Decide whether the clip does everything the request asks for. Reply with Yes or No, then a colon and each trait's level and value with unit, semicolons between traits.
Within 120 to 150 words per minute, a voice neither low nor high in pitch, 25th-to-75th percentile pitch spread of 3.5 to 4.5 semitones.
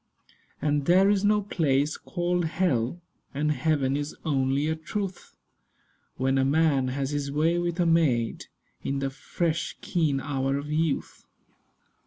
Yes: average, 145 wpm; medium, 150 Hz; average, 3.8 semitones